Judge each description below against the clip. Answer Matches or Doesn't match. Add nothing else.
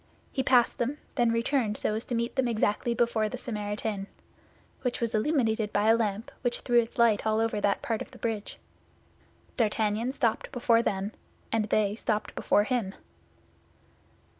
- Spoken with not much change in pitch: Matches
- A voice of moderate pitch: Doesn't match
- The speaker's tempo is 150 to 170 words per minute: Matches